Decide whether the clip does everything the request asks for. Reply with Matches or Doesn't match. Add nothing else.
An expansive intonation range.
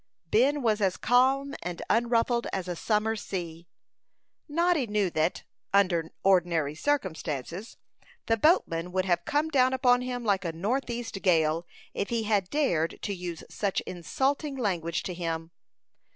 Matches